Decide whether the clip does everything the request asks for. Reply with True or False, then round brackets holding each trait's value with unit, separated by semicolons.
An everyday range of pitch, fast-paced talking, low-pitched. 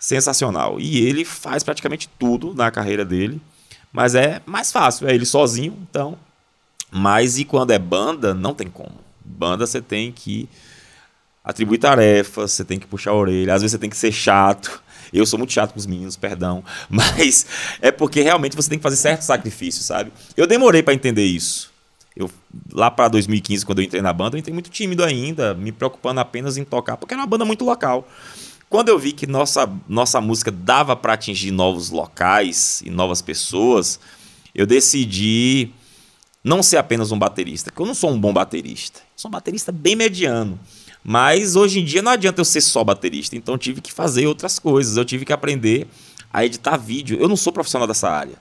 False (6.3 semitones; 195 wpm; 125 Hz)